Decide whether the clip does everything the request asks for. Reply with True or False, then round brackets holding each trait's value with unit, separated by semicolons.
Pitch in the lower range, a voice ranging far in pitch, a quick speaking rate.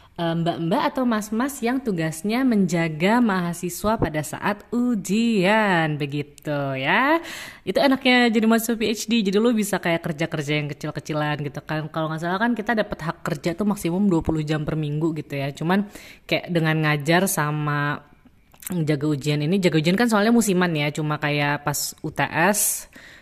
False (170 Hz; 5.8 semitones; 155 wpm)